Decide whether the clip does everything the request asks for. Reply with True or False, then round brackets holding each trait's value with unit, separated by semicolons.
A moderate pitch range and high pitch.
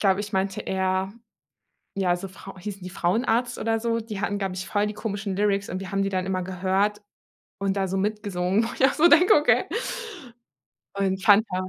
False (2.0 semitones; 195 Hz)